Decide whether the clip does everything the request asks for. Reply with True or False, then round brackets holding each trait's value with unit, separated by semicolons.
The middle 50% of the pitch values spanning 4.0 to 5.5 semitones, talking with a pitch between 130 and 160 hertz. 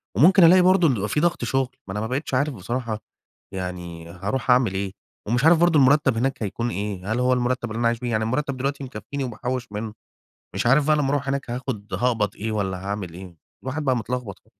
False (4.6 semitones; 120 Hz)